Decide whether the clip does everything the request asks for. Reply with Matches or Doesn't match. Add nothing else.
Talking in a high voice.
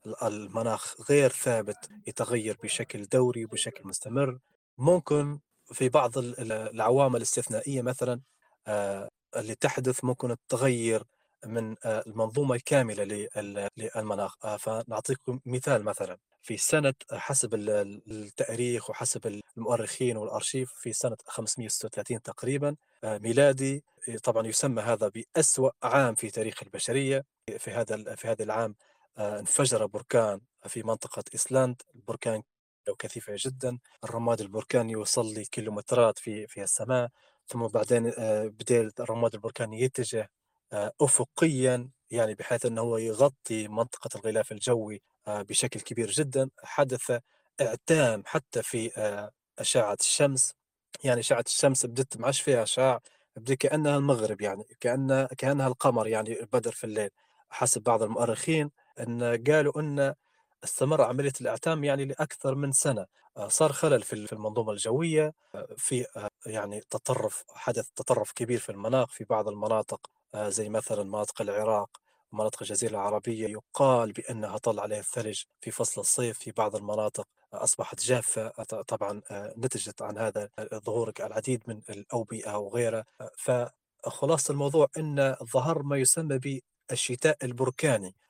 Doesn't match